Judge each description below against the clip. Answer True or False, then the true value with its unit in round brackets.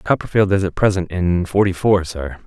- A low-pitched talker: True (90 Hz)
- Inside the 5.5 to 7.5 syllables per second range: False (5.0 syllables/s)